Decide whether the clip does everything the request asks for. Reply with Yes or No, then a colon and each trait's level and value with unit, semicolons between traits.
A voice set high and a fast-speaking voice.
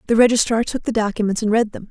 Yes: high, 220 Hz; fast, 250 wpm